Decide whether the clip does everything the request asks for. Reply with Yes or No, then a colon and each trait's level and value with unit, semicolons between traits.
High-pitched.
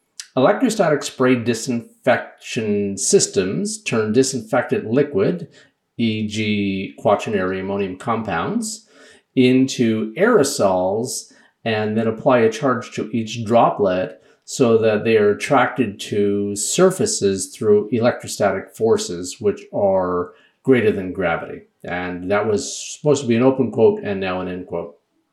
No: low, 115 Hz